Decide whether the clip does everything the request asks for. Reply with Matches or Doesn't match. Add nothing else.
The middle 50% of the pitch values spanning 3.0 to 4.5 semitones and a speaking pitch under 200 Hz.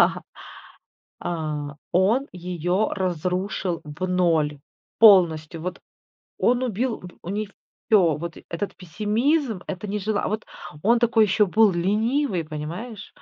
Matches